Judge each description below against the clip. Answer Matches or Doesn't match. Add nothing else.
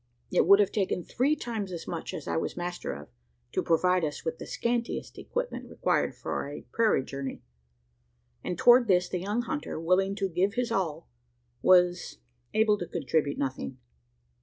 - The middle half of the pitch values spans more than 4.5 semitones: Matches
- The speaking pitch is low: Doesn't match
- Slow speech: Doesn't match